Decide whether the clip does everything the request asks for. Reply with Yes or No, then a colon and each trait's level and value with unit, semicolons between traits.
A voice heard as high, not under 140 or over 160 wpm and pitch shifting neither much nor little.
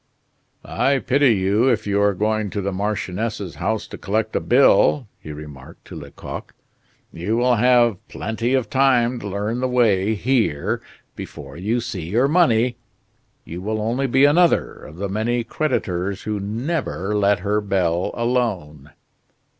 No: low, 110 Hz; average, 155 wpm; average, 3.8 semitones